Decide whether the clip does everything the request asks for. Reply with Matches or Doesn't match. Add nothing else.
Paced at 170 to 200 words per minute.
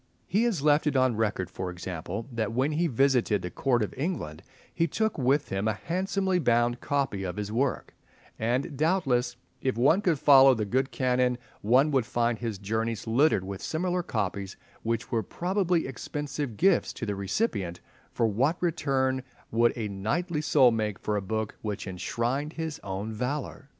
Matches